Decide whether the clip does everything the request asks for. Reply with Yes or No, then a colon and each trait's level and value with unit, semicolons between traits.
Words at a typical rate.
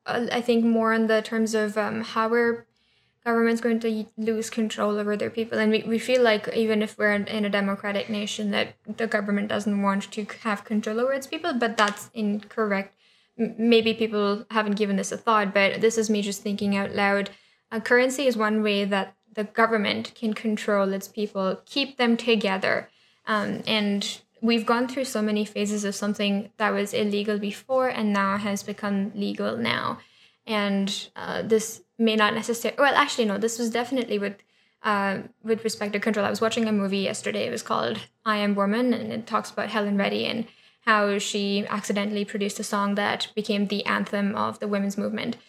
Yes: average, 195 wpm